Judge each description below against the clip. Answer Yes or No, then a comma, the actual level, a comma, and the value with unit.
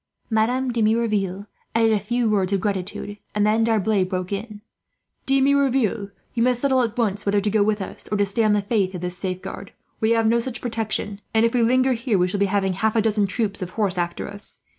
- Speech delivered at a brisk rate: Yes, fast, 230 wpm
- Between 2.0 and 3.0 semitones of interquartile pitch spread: Yes, narrow, 2.6 semitones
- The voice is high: Yes, high, 215 Hz